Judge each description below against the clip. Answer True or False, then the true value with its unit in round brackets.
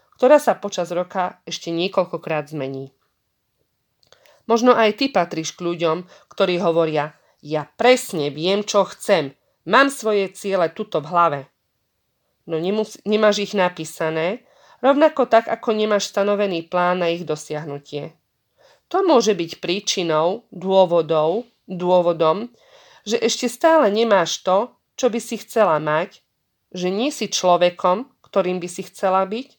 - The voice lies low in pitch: False (185 Hz)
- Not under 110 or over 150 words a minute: True (130 wpm)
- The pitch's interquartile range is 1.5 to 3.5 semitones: False (4.9 semitones)